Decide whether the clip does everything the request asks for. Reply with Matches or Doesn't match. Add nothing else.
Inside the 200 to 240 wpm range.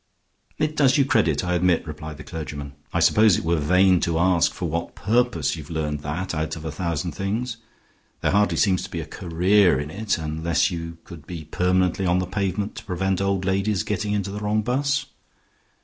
Matches